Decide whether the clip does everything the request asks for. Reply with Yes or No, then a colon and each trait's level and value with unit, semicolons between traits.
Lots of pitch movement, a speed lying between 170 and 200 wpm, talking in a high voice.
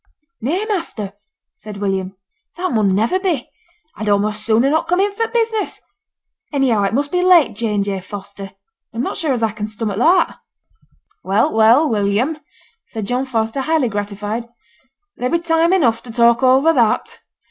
Yes: wide, 7.3 semitones; average, 175 wpm; high, 235 Hz